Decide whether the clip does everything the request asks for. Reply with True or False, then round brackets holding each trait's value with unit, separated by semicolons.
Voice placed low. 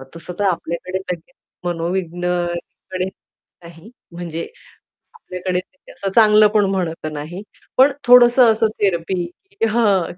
False (185 Hz)